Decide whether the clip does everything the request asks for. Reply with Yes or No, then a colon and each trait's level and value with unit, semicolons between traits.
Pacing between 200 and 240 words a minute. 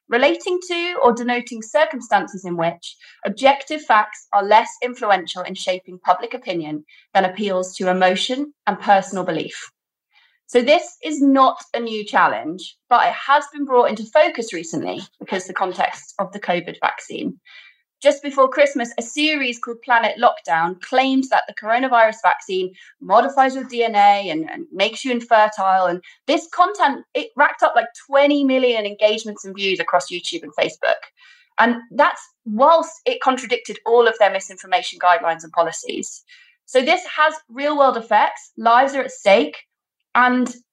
No: average, 155 wpm